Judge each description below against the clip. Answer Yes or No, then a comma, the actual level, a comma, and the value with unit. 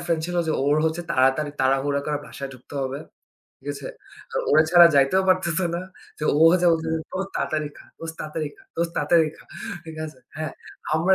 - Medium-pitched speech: Yes, medium, 155 Hz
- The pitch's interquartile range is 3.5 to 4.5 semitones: No, average, 2.8 semitones